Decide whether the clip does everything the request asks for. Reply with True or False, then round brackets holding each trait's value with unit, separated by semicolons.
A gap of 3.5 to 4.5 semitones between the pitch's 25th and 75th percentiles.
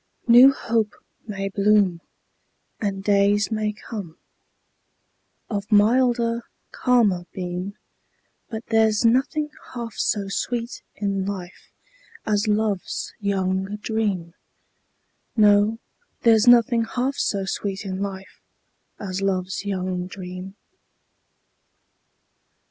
False (2.7 semitones)